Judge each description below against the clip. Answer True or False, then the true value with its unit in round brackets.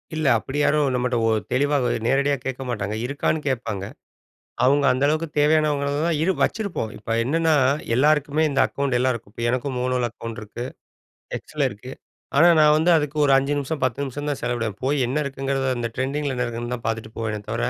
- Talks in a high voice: False (135 Hz)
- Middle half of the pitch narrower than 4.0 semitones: True (3.5 semitones)